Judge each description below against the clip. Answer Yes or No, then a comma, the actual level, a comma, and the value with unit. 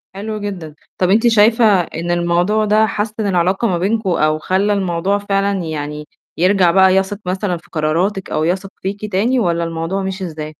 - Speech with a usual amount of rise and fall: Yes, average, 3.3 semitones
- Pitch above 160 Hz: Yes, high, 190 Hz